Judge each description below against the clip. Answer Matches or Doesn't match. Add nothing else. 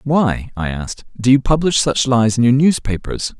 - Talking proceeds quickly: Doesn't match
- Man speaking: Matches